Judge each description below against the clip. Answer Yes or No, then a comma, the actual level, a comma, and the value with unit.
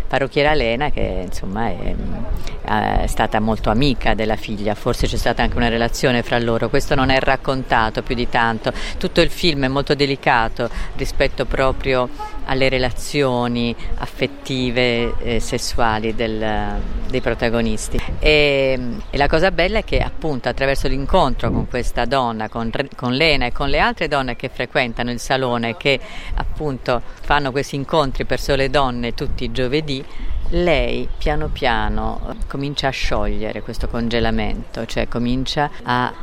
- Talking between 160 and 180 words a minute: No, average, 145 wpm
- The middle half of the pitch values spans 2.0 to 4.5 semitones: Yes, average, 3.1 semitones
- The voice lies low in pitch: Yes, low, 125 Hz